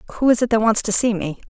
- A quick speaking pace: Yes, fast, 320 wpm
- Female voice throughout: Yes, female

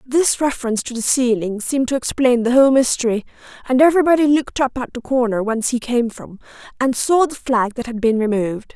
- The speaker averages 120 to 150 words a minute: No, fast, 205 wpm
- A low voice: No, very high, 250 Hz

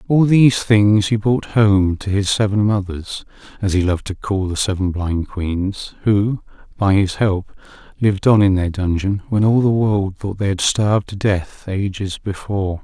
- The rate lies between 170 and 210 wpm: Yes, average, 185 wpm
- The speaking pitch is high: No, low, 100 Hz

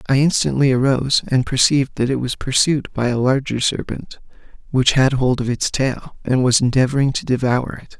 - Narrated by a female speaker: No, male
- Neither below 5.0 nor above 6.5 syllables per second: Yes, 5.4 syllables/s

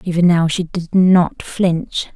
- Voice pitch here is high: No, medium, 175 Hz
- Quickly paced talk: No, average, 165 wpm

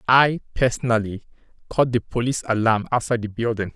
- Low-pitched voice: Yes, low, 115 Hz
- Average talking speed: Yes, average, 145 wpm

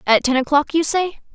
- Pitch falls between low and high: No, very high, 295 Hz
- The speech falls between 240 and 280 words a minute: No, fast, 225 wpm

